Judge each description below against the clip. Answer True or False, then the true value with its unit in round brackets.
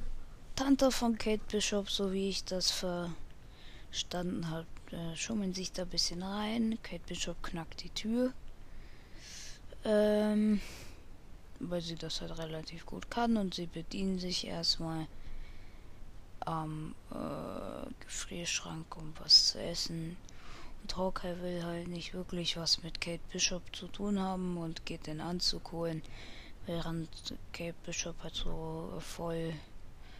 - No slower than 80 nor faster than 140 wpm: True (130 wpm)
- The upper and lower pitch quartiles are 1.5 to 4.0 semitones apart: True (3.2 semitones)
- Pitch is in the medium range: True (170 Hz)